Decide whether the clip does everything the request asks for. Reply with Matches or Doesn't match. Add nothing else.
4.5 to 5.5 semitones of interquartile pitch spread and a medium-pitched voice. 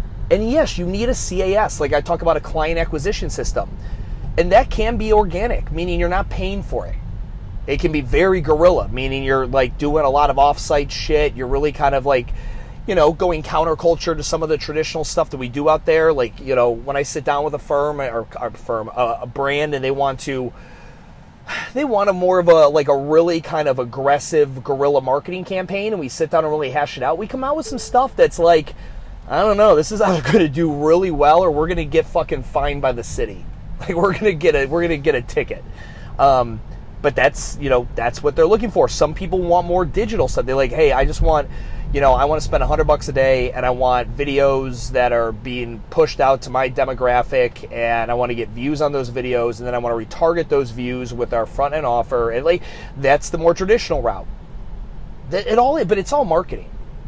Matches